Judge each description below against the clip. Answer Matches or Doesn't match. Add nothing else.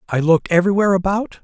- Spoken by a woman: Doesn't match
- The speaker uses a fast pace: Doesn't match